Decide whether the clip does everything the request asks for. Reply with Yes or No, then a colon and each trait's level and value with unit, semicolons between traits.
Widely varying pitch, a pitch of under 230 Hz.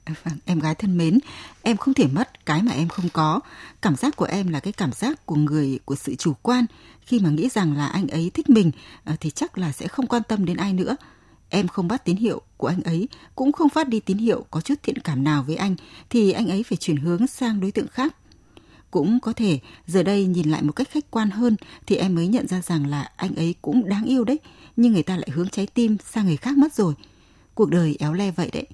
Yes: wide, 6.5 semitones; high, 190 Hz